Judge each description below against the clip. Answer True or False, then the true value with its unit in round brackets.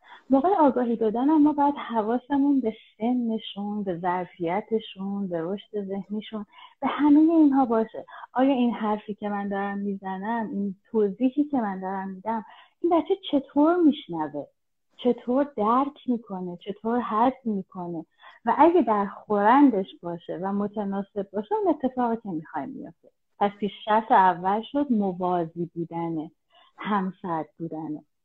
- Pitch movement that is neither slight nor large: True (4.9 semitones)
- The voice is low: False (215 Hz)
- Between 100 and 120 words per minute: False (130 wpm)